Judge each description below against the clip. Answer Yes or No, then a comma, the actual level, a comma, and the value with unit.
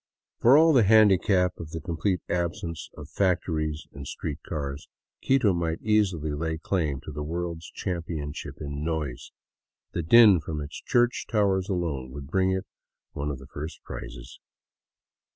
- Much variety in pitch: No, average, 4.2 semitones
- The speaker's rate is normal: Yes, average, 150 wpm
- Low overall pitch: Yes, very low, 85 Hz